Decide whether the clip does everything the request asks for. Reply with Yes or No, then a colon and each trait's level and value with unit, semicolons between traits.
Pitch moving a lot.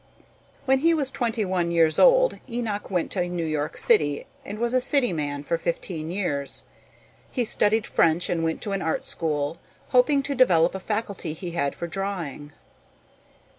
Yes: wide, 6.2 semitones